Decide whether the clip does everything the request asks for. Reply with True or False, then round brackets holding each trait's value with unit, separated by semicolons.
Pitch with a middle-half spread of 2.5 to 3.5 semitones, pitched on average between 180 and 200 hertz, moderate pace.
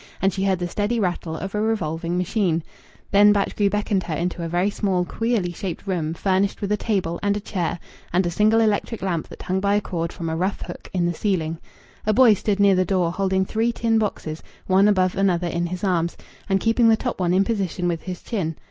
False (3.0 semitones; 190 Hz; 230 wpm)